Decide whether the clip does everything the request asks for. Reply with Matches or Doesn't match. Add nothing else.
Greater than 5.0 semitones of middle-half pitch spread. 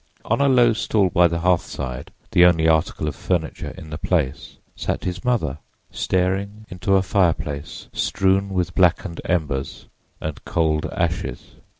Doesn't match